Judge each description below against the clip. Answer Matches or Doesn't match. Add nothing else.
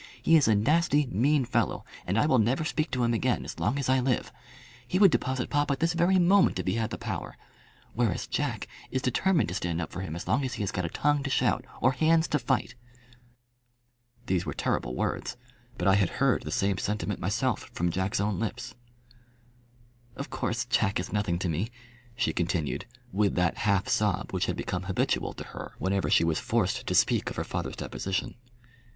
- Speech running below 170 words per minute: Doesn't match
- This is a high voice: Doesn't match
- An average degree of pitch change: Doesn't match